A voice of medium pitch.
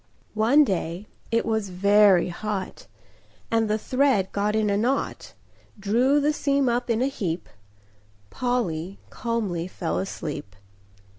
No: high, 215 Hz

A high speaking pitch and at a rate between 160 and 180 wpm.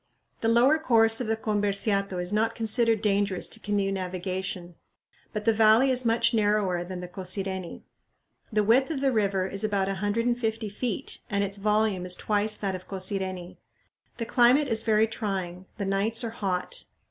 Yes: high, 205 Hz; average, 170 wpm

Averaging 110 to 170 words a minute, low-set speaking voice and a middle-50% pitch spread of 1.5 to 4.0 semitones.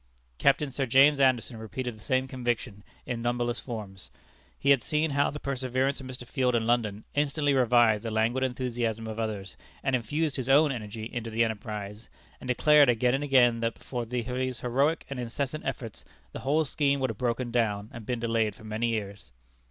No: average, 190 wpm; low, 120 Hz; average, 3.1 semitones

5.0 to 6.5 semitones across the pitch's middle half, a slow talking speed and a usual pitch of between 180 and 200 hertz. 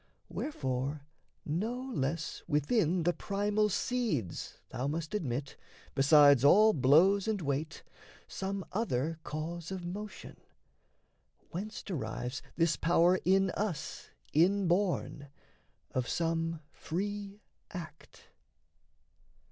No: average, 5.3 semitones; slow, 95 wpm; medium, 170 Hz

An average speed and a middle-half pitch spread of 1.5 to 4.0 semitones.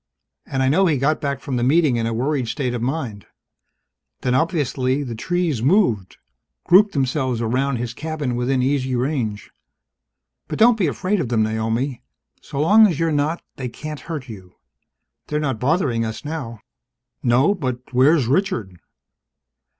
No: average, 160 wpm; average, 4.5 semitones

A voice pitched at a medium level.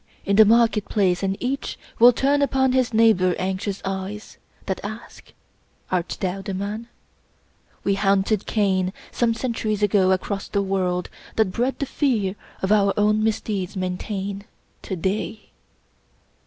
No: high, 200 Hz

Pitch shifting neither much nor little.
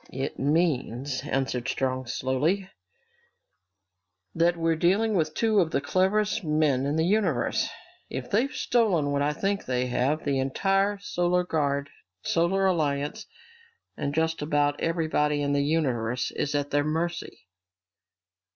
Yes: average, 4.1 semitones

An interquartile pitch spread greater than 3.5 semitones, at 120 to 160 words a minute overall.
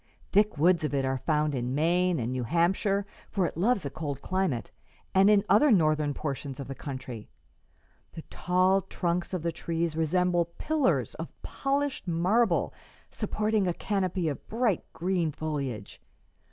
Yes: average, 4.5 semitones; average, 155 wpm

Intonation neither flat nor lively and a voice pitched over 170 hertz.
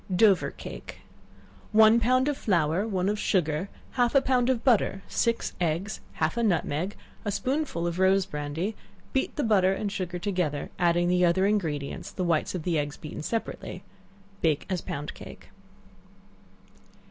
Yes: average, 4.7 semitones; high, 190 Hz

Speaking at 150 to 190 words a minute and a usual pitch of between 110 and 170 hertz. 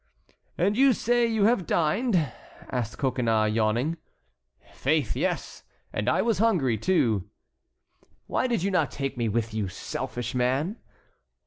No: slow, 135 wpm; low, 135 Hz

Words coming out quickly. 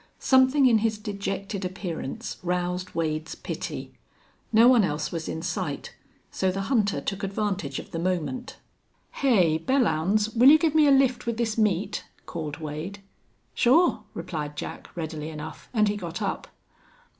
No: average, 155 wpm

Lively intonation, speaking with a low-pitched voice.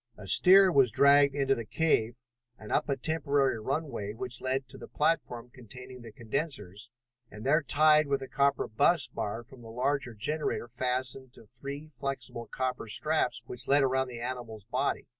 No: average, 3.2 semitones; low, 130 Hz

